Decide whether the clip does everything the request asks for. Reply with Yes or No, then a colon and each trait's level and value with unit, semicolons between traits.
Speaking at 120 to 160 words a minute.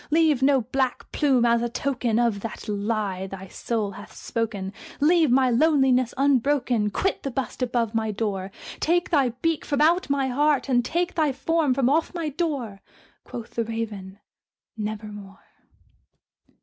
Yes: average, 155 wpm